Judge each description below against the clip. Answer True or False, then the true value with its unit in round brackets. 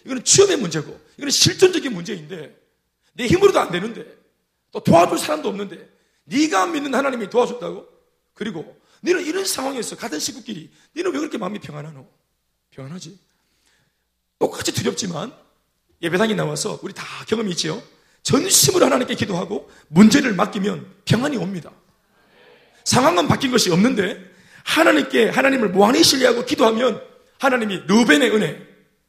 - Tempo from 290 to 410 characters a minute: True (345 characters per minute)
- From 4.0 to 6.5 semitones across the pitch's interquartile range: False (7.1 semitones)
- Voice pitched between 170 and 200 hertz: False (225 Hz)